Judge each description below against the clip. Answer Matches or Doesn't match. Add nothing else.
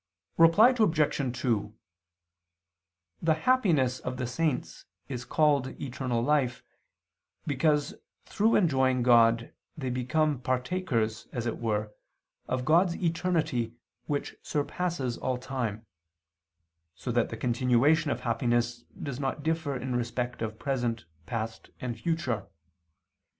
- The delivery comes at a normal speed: Doesn't match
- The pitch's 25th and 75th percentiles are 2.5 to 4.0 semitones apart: Doesn't match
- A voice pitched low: Matches